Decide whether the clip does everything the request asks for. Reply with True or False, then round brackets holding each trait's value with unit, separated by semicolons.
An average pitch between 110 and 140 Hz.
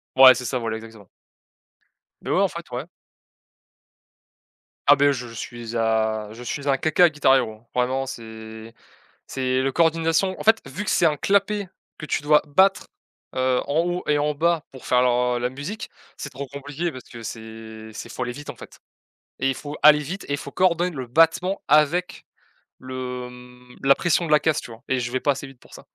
True (135 Hz)